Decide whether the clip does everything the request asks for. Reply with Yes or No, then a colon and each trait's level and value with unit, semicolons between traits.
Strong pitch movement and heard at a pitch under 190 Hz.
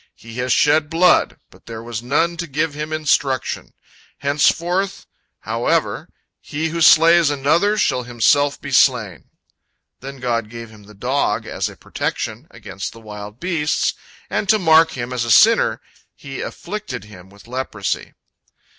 Yes: wide, 5.8 semitones; low, 135 Hz